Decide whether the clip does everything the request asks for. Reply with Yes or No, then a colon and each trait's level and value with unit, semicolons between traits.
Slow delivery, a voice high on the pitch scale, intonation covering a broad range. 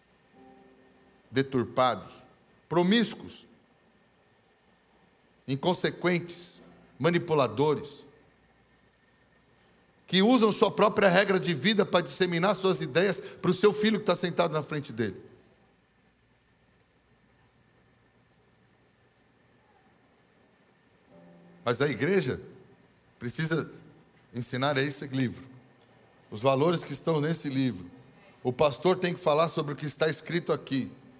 No: slow, 95 wpm; medium, 150 Hz; wide, 5.8 semitones